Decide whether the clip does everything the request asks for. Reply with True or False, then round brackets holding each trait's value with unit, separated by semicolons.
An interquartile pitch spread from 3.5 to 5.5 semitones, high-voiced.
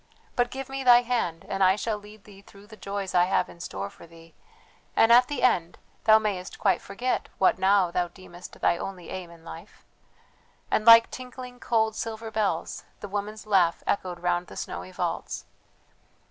True (4.2 semitones; 200 Hz)